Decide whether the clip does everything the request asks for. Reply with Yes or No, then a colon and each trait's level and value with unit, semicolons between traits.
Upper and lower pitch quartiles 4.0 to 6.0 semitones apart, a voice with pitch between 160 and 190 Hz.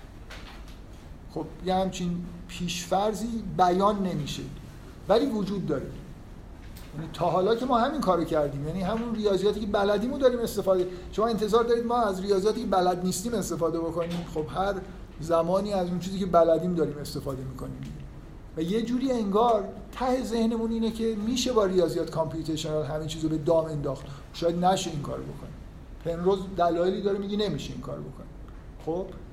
Yes: average, 4.7 semitones; medium, 185 Hz